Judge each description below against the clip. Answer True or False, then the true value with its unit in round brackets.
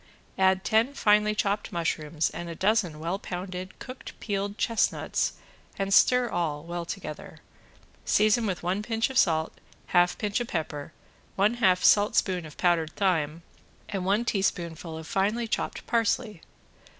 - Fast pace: False (145 wpm)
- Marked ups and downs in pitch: False (3.9 semitones)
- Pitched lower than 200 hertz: True (190 Hz)